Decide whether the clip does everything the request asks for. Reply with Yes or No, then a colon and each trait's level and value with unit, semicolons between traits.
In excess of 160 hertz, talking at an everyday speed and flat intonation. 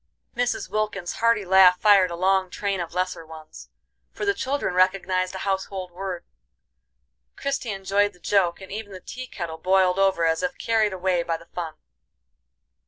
Yes: high, 190 Hz; average, 170 wpm; narrow, 2.3 semitones